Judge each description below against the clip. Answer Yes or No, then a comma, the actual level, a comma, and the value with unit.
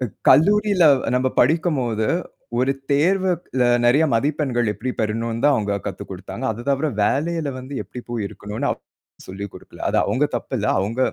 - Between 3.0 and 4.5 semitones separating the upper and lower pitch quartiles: No, average, 5.2 semitones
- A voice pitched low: Yes, low, 130 Hz